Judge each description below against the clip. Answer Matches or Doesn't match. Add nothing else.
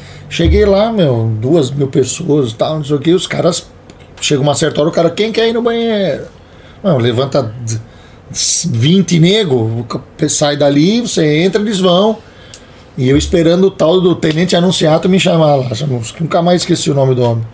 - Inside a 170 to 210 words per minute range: Matches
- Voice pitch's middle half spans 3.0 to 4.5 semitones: Doesn't match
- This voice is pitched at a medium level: Matches